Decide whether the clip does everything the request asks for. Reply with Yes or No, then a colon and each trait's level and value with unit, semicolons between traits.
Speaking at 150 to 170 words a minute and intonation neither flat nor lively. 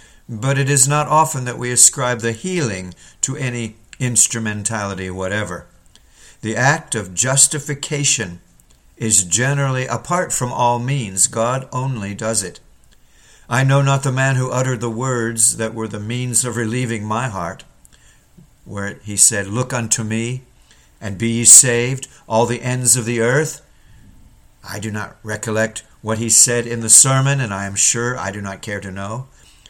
Yes: average, 165 wpm; average, 3.4 semitones